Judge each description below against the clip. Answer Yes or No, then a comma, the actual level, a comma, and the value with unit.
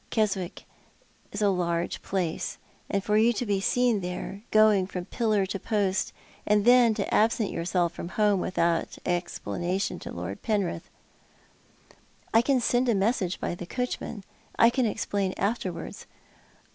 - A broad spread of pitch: No, average, 3.5 semitones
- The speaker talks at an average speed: Yes, average, 150 wpm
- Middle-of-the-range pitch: No, high, 200 Hz